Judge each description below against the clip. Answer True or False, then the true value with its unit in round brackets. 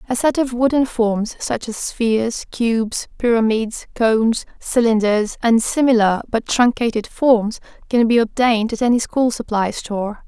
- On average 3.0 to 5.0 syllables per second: True (4.5 syllables/s)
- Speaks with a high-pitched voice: True (230 Hz)